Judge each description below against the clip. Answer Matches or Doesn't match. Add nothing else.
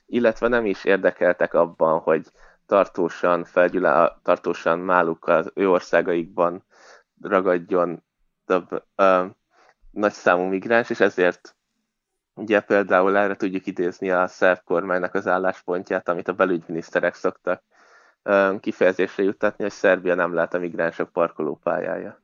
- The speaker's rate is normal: Matches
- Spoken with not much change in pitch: Matches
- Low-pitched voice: Matches